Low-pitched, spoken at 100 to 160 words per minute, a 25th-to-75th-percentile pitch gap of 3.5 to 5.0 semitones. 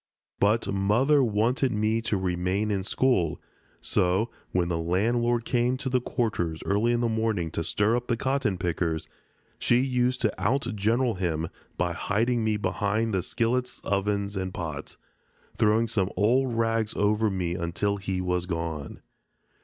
Yes: low, 105 Hz; average, 155 wpm; average, 4.3 semitones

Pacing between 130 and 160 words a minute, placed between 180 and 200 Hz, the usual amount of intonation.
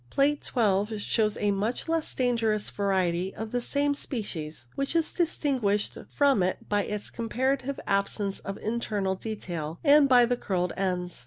No: average, 155 wpm; high, 215 Hz; average, 5.0 semitones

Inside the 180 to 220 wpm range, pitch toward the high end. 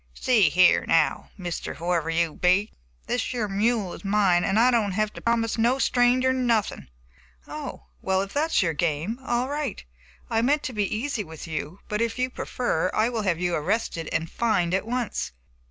Yes: average, 190 wpm; high, 210 Hz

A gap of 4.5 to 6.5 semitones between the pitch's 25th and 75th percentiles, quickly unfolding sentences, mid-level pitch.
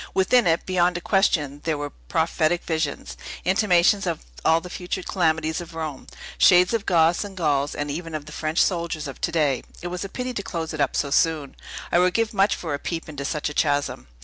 No: average, 3.0 semitones; fast, 220 wpm; medium, 165 Hz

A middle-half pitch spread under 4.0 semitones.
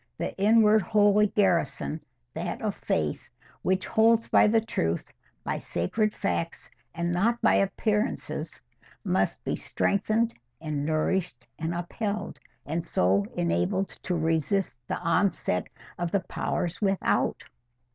No: average, 4.6 semitones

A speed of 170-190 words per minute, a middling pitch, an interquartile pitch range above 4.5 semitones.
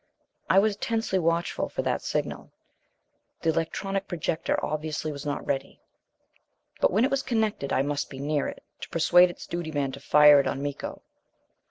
Yes: average, 175 wpm; medium, 160 Hz; average, 4.9 semitones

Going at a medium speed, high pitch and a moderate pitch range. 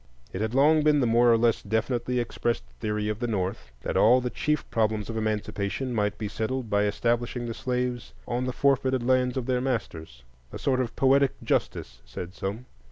No: average, 190 wpm; low, 120 Hz; average, 3.4 semitones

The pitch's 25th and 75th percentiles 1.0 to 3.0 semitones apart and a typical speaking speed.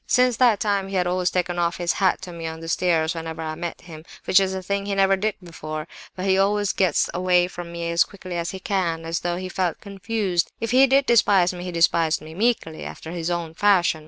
No: average, 2.7 semitones; fast, 245 wpm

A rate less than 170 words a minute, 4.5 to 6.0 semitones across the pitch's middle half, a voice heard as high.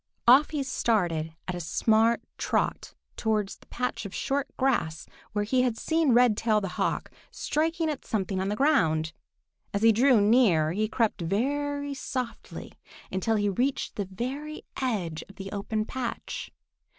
Yes: average, 155 wpm; average, 5.3 semitones; high, 225 Hz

